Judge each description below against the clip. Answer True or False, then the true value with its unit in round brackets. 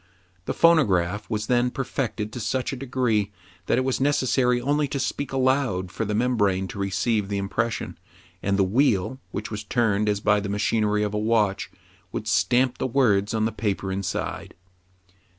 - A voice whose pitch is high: False (110 Hz)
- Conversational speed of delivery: True (175 wpm)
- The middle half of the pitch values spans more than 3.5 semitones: True (4.0 semitones)